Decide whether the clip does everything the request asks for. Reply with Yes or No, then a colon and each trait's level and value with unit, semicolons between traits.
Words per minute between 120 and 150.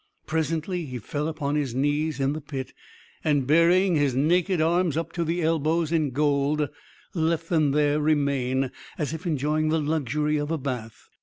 No: average, 170 wpm